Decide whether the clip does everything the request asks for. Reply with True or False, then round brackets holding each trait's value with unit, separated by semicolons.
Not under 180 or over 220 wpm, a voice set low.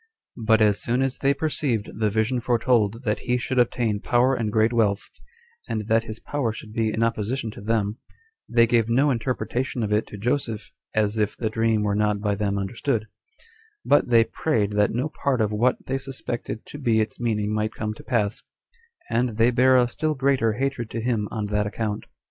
True (200 wpm; 115 Hz)